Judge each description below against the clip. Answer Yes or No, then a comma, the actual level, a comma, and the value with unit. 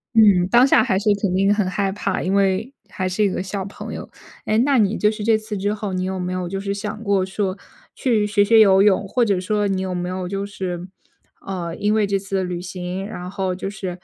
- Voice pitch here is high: Yes, high, 195 Hz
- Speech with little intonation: Yes, narrow, 2.0 semitones